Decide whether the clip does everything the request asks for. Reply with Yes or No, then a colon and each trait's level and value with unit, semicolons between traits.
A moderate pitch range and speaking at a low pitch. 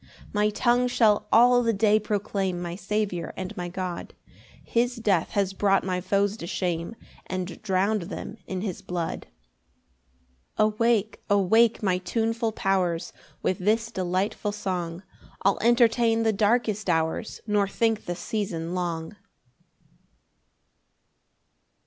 No: average, 3.4 semitones; high, 200 Hz